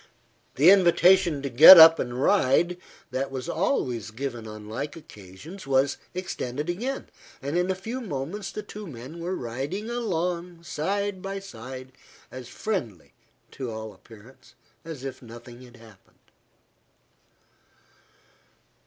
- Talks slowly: Yes, slow, 130 wpm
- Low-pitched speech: No, medium, 145 Hz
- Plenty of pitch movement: Yes, wide, 7.1 semitones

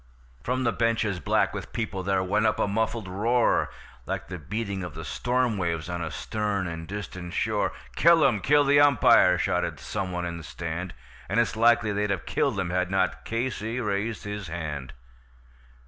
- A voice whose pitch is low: Yes, low, 100 Hz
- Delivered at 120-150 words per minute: No, average, 185 wpm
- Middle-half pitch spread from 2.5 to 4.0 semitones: No, average, 4.4 semitones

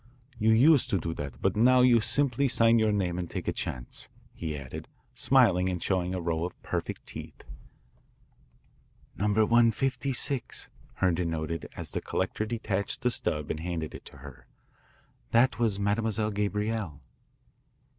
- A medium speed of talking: Yes, average, 150 wpm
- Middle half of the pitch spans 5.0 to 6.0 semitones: Yes, wide, 5.4 semitones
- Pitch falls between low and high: No, low, 105 Hz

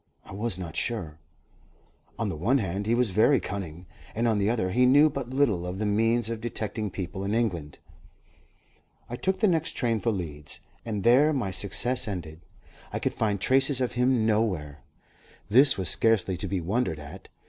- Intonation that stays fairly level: No, average, 4.8 semitones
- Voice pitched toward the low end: Yes, low, 110 Hz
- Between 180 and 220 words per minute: Yes, average, 185 wpm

